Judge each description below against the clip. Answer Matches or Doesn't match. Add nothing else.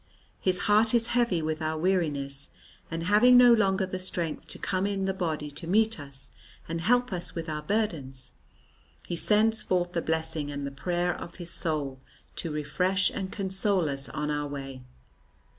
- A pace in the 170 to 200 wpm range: Matches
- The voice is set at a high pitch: Doesn't match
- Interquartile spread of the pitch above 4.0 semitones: Matches